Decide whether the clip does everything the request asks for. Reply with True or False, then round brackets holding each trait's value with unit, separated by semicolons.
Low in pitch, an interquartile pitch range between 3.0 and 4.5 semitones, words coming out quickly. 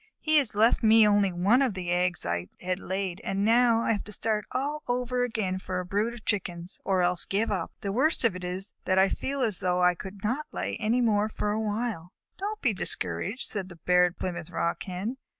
False (205 Hz; 4.2 semitones; 220 wpm)